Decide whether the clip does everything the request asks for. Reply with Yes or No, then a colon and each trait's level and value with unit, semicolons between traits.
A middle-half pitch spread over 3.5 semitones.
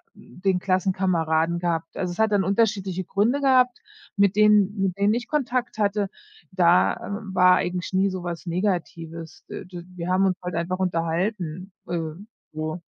No: average, 2.9 semitones